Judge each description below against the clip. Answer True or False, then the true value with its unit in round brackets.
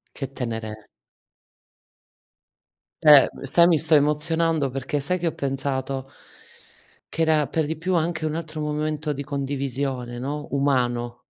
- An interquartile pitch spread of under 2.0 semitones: False (2.8 semitones)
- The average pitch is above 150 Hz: False (145 Hz)